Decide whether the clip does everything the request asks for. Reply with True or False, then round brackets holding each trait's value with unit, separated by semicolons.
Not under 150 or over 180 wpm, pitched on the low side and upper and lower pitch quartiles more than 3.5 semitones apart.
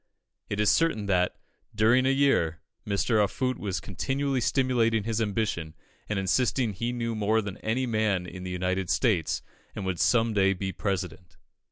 True (170 wpm; 105 Hz; 3.9 semitones)